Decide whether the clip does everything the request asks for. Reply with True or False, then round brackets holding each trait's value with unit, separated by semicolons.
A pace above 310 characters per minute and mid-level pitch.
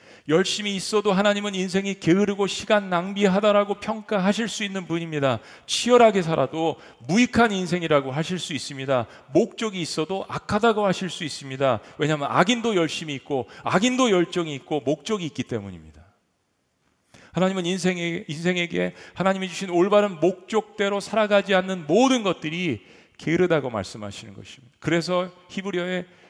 True (365 characters per minute; 180 Hz)